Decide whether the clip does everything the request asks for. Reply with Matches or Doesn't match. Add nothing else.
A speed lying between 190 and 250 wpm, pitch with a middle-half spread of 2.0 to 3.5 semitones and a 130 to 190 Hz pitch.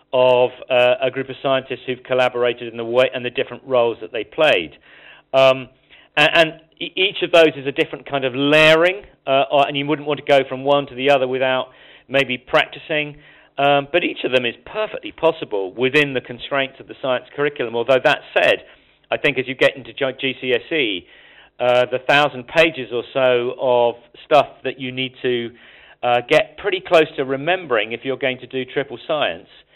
Matches